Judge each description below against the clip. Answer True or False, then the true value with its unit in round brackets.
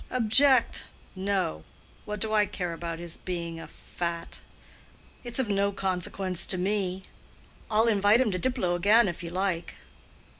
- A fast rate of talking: False (150 wpm)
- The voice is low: False (195 Hz)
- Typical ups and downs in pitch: True (3.5 semitones)